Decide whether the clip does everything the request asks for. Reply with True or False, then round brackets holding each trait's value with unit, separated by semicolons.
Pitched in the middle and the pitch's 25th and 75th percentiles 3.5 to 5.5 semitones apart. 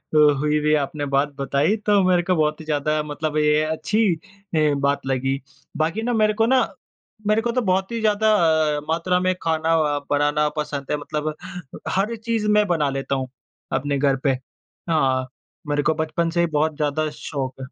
True (155 Hz; 4.3 semitones)